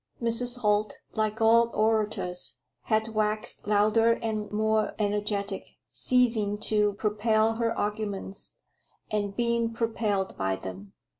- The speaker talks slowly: Yes, slow, 115 wpm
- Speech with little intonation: Yes, narrow, 1.6 semitones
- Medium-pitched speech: No, high, 215 Hz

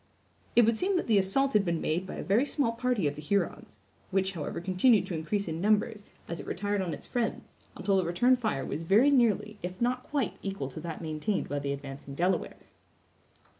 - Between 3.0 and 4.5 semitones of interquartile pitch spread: No, wide, 5.6 semitones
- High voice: Yes, high, 195 Hz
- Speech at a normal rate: No, fast, 210 wpm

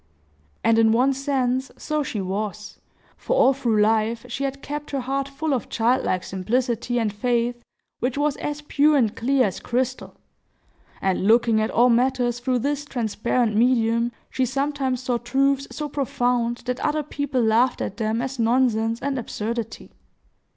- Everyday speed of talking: Yes, average, 160 wpm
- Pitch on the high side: Yes, high, 245 Hz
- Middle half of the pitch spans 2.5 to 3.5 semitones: Yes, average, 3.2 semitones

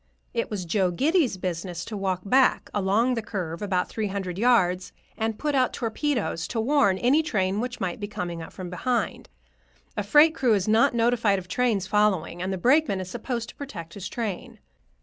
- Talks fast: No, average, 190 wpm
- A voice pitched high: Yes, high, 205 Hz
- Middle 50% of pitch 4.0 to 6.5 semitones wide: Yes, average, 4.8 semitones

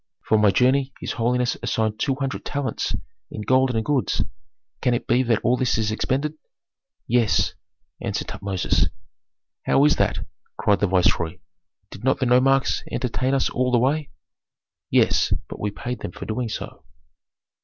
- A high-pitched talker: No, low, 125 Hz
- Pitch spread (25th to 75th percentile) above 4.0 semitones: No, average, 3.3 semitones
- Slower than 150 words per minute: No, average, 160 wpm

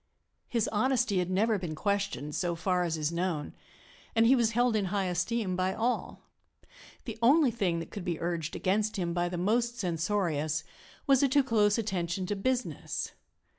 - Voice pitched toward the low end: No, high, 195 Hz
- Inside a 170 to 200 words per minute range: Yes, average, 175 wpm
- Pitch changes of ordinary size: Yes, average, 4.7 semitones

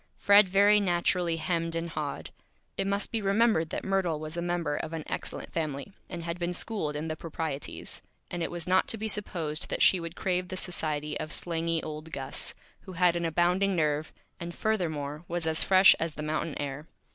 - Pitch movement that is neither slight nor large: Yes, average, 3.0 semitones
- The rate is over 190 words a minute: Yes, average, 200 wpm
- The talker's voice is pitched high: No, medium, 170 Hz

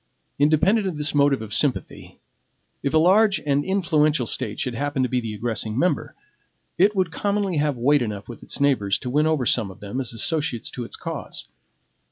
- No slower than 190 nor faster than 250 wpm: Yes, average, 195 wpm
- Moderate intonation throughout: Yes, average, 5.0 semitones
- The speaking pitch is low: No, medium, 145 Hz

